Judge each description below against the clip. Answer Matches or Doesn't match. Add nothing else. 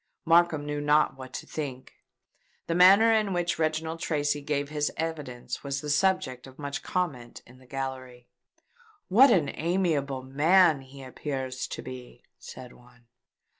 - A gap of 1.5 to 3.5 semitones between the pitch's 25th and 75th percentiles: Doesn't match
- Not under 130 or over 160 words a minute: Matches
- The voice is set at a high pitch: Doesn't match